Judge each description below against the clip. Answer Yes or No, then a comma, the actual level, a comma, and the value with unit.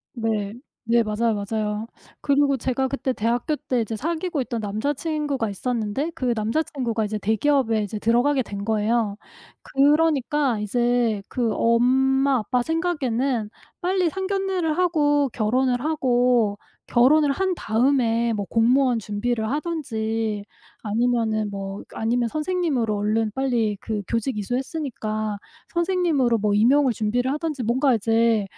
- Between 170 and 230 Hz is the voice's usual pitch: No, high, 240 Hz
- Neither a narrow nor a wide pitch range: Yes, average, 4.6 semitones